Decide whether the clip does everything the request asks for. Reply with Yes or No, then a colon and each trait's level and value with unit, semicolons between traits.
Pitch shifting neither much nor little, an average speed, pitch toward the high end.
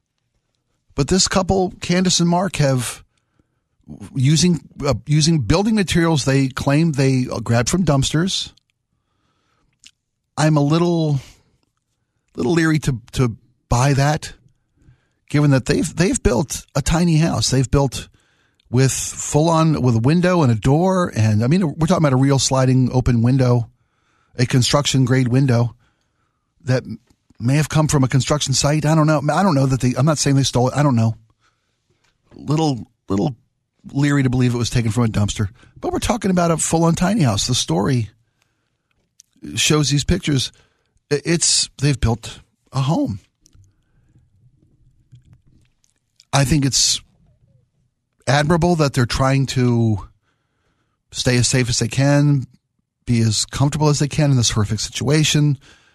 No: average, 3.7 semitones; average, 150 wpm; low, 135 Hz